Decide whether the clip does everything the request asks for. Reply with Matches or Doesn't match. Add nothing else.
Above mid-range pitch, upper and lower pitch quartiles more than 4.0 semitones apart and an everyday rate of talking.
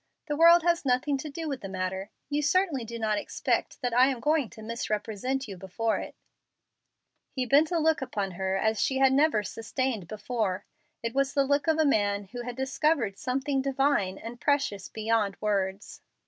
Matches